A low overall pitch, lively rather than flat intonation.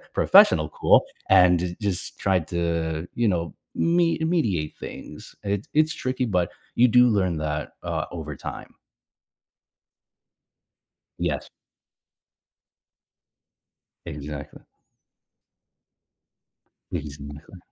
Yes: very low, 90 Hz; wide, 6.6 semitones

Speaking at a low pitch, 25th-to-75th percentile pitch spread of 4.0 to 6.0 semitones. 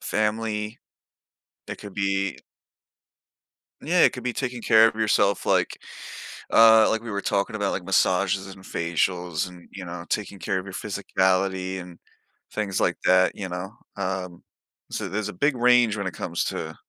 No: low, 100 Hz; average, 2.8 semitones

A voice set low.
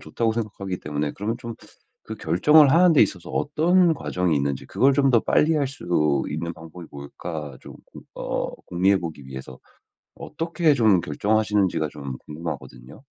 Yes: very low, 95 Hz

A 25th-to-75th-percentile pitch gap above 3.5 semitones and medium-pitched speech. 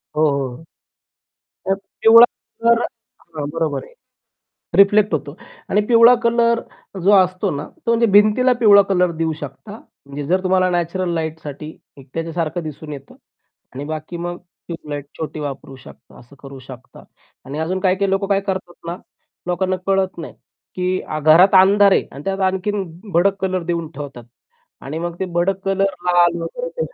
Yes: average, 4.0 semitones; medium, 175 Hz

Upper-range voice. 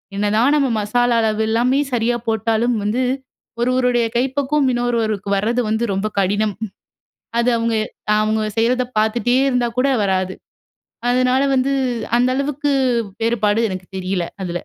Yes: high, 235 Hz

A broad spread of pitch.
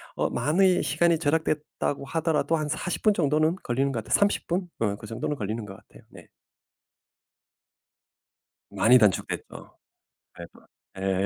Yes: wide, 6.6 semitones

